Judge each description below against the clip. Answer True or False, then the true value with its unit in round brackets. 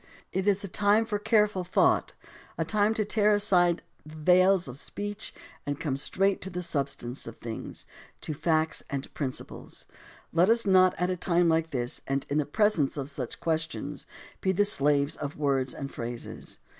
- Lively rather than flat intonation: True (5.9 semitones)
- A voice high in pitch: False (170 Hz)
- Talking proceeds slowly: False (185 wpm)